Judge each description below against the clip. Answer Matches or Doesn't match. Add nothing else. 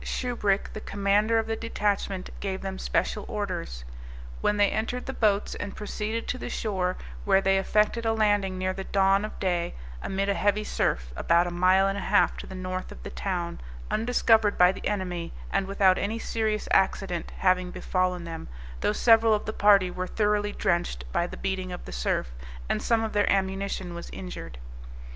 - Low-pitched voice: Doesn't match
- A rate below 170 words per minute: Doesn't match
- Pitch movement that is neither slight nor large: Doesn't match